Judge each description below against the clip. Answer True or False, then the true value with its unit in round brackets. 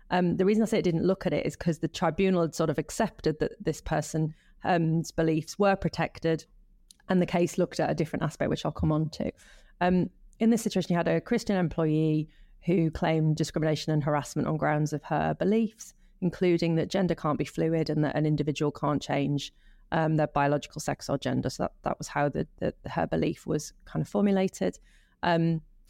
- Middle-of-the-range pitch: True (165 Hz)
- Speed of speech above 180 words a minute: True (205 wpm)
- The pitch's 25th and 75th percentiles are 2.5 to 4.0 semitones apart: True (2.9 semitones)